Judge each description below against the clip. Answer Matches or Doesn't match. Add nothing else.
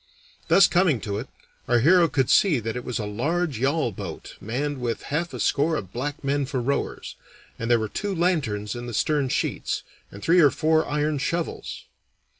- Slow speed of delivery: Doesn't match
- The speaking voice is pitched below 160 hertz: Matches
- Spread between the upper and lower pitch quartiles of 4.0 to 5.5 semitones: Matches